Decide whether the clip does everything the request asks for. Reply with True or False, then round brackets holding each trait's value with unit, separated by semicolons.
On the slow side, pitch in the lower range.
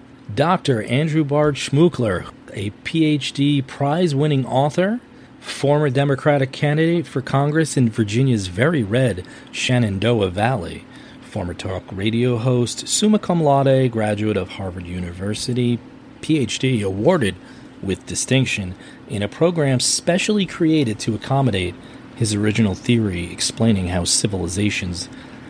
True (115 wpm; 125 Hz)